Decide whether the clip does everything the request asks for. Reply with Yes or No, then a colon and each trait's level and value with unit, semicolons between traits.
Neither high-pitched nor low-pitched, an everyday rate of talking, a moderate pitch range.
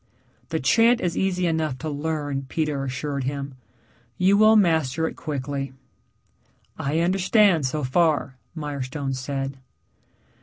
No: medium, 150 Hz; slow, 120 wpm; average, 3.7 semitones